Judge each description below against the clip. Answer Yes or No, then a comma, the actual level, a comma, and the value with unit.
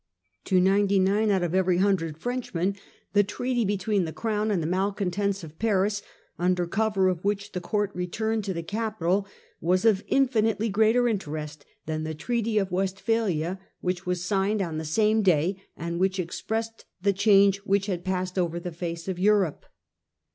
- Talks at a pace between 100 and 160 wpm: No, average, 175 wpm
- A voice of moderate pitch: No, high, 195 Hz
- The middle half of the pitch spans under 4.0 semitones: Yes, average, 2.9 semitones